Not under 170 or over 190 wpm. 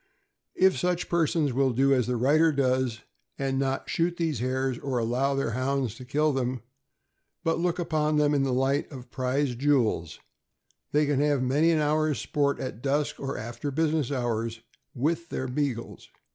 Yes: average, 175 wpm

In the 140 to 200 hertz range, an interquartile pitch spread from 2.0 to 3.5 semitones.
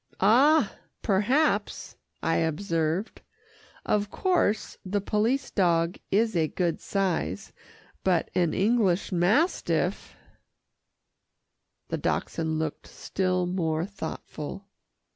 No: high, 190 Hz; average, 4.1 semitones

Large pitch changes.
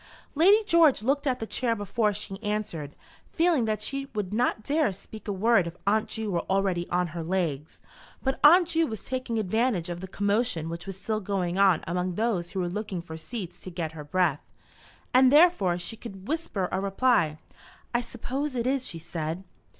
Yes: wide, 5.8 semitones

